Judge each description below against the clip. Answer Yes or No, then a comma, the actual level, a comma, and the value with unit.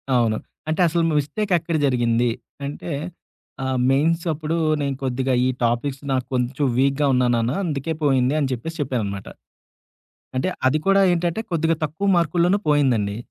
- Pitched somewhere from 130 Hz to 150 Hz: Yes, medium, 140 Hz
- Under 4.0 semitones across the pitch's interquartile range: No, average, 4.4 semitones